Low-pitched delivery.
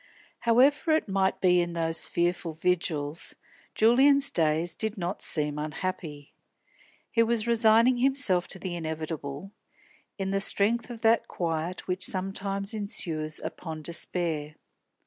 No: medium, 185 Hz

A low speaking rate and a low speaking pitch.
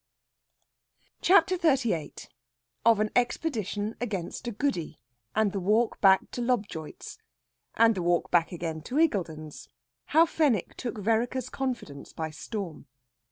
No: slow, 125 wpm; high, 215 Hz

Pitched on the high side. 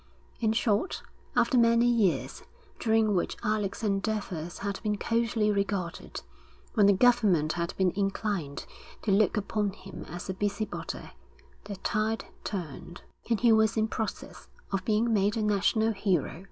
Yes: high, 210 Hz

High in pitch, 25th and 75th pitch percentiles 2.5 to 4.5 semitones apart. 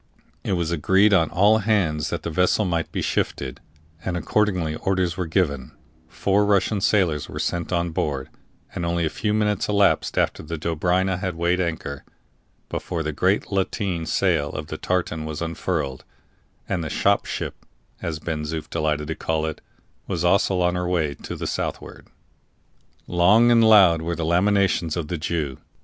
No: very low, 85 Hz; average, 3.2 semitones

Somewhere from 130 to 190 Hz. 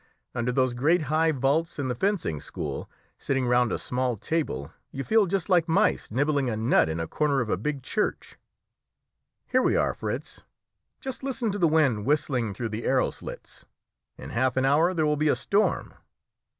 Yes: medium, 140 Hz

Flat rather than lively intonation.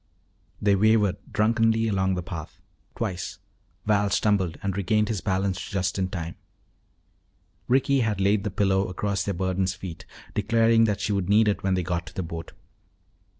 Yes: narrow, 2.3 semitones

